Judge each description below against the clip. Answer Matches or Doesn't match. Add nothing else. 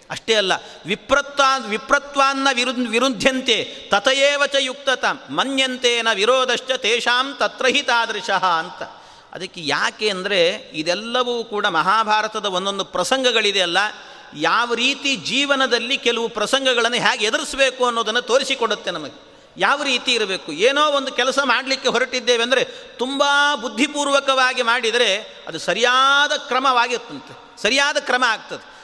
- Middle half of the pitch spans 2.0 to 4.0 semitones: Matches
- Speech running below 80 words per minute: Doesn't match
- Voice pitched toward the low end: Doesn't match